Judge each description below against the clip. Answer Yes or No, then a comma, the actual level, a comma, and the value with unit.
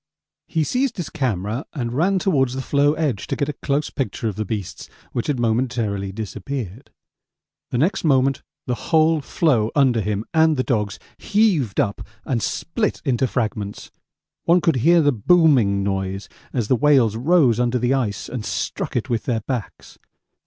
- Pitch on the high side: No, low, 125 Hz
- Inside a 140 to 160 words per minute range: No, average, 170 wpm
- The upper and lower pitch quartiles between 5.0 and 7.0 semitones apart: Yes, average, 5.3 semitones